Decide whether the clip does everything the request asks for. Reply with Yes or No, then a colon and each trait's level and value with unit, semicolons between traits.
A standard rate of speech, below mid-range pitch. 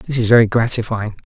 Yes: average, 190 wpm; low, 115 Hz